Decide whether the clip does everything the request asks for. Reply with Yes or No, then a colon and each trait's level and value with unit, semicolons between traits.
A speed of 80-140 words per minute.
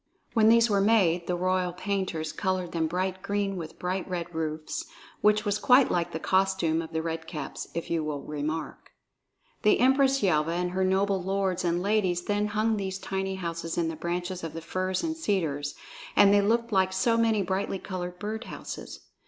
No: average, 190 wpm